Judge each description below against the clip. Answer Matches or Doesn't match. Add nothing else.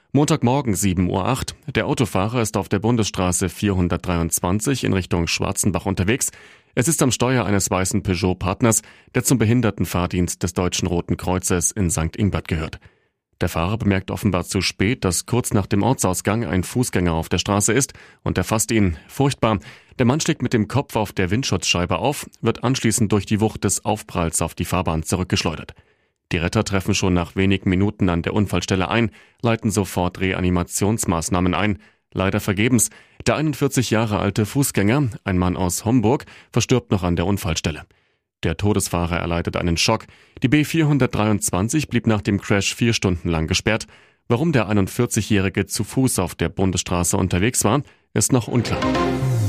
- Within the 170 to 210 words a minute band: Doesn't match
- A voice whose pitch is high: Doesn't match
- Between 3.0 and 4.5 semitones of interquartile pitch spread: Matches